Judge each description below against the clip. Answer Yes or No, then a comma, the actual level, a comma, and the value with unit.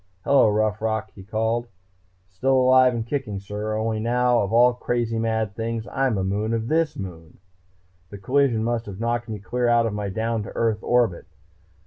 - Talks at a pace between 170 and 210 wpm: Yes, average, 185 wpm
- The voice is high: No, low, 115 Hz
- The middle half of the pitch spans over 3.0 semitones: No, narrow, 2.5 semitones